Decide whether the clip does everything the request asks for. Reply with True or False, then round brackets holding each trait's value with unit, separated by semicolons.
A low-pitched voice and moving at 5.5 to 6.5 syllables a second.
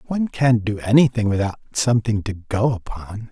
True (115 Hz; 5.6 syllables/s)